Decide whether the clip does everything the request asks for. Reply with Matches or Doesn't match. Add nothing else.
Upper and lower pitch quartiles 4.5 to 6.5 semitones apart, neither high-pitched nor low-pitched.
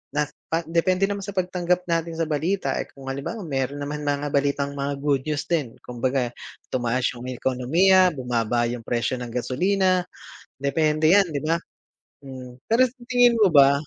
Matches